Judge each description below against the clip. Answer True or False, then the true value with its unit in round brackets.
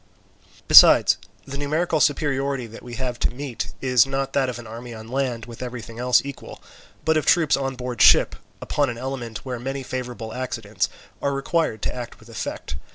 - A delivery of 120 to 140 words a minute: False (185 wpm)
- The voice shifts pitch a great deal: False (2.5 semitones)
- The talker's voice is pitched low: True (125 Hz)